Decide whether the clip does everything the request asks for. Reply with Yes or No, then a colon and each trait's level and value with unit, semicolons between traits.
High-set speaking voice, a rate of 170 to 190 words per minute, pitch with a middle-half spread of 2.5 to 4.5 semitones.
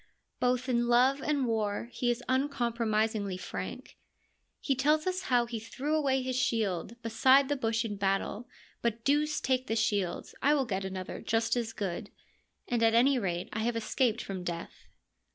Yes: high, 235 Hz; average, 175 wpm; average, 3.3 semitones